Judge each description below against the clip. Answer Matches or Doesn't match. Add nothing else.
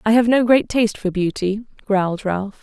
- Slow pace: Doesn't match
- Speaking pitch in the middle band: Doesn't match